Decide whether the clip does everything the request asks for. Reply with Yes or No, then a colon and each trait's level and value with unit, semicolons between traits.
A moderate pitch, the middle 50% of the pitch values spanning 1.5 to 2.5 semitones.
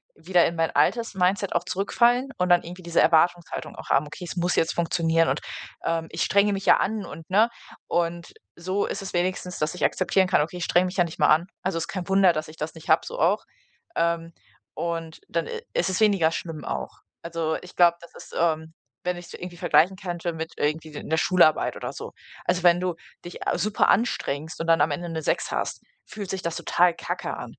Yes: medium, 175 Hz; narrow, 2.2 semitones